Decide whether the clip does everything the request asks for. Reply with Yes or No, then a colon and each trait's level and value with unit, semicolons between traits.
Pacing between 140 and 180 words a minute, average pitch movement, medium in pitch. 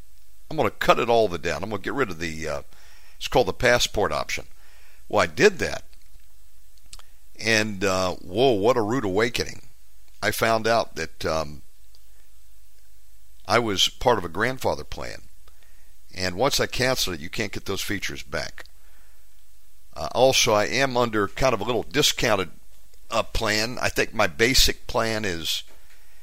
No: average, 165 wpm; average, 3.3 semitones; low, 100 Hz